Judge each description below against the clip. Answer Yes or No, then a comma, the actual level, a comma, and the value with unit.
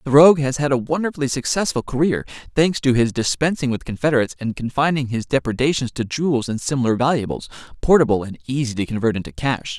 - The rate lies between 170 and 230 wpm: Yes, average, 185 wpm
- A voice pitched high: No, low, 130 Hz